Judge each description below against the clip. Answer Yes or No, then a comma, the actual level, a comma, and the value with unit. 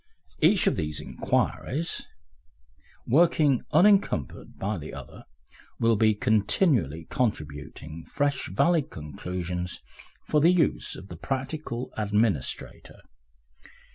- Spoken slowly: Yes, slow, 100 wpm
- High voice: No, low, 110 Hz